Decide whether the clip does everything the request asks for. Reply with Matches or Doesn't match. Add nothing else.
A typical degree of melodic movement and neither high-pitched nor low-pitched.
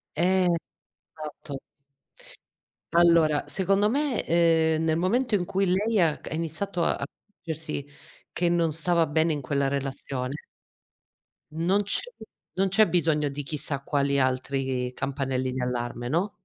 Matches